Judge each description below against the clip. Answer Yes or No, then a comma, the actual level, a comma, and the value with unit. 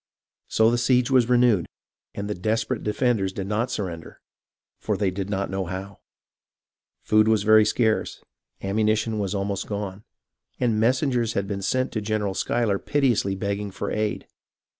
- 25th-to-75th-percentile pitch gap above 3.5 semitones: No, average, 2.9 semitones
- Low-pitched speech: Yes, low, 105 Hz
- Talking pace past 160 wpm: No, average, 155 wpm